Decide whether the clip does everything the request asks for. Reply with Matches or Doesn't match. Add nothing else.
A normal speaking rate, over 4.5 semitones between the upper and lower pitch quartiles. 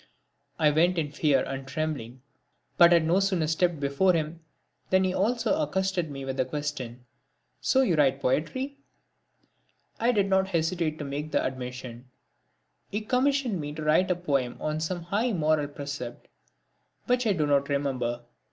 Matches